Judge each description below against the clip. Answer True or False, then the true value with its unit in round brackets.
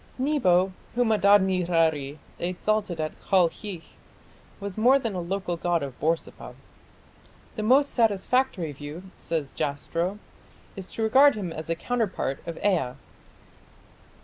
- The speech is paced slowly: True (125 wpm)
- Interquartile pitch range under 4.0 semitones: False (4.7 semitones)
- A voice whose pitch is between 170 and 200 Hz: True (185 Hz)